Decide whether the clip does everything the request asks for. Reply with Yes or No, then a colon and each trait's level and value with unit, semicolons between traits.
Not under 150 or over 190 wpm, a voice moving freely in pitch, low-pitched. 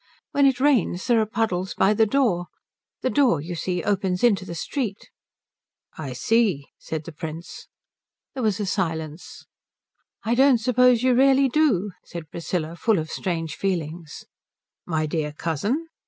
No: average, 155 wpm; wide, 6.6 semitones; high, 190 Hz